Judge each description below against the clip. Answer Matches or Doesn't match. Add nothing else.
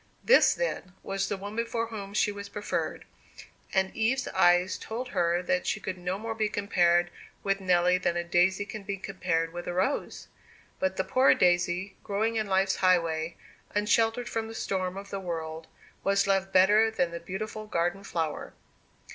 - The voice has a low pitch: Doesn't match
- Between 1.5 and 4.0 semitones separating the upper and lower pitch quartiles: Matches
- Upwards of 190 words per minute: Doesn't match